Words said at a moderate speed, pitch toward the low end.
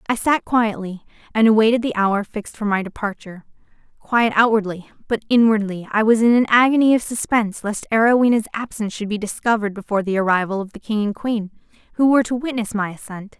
No: average, 185 wpm; high, 215 Hz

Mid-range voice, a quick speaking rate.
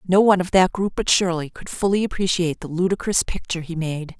Yes: medium, 180 Hz; fast, 215 wpm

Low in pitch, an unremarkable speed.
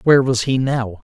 No: low, 125 Hz; fast, 215 wpm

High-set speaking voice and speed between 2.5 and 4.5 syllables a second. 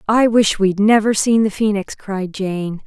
Yes: high, 205 Hz; 4.1 syllables/s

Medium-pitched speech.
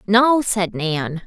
No: high, 200 Hz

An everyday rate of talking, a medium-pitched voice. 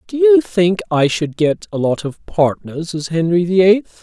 No: fast, 210 wpm; medium, 180 Hz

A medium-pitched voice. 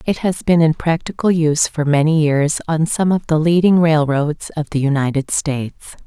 Yes: medium, 155 Hz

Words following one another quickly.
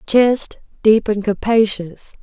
No: slow, 80 wpm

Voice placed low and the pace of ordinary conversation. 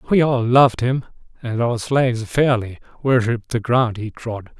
Yes: low, 120 Hz; average, 170 wpm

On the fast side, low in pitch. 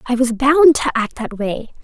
No: fast, 230 wpm; very high, 250 Hz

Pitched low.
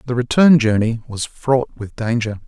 Yes: low, 120 Hz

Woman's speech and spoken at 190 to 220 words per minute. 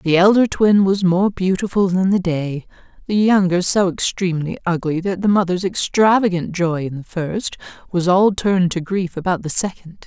No: female; average, 175 wpm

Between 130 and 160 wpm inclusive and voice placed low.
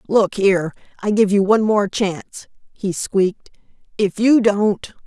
No: average, 155 wpm; high, 200 Hz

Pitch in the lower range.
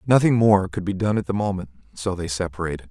Yes: very low, 95 Hz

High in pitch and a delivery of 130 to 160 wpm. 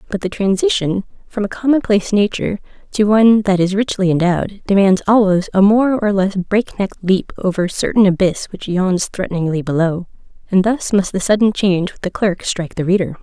No: high, 195 Hz; average, 185 wpm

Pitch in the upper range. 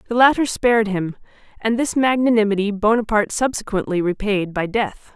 Yes: high, 215 Hz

